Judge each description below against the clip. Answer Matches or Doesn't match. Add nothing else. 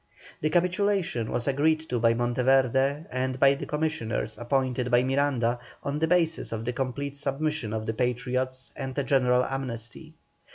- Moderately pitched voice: Doesn't match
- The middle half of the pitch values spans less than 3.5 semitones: Matches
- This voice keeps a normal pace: Matches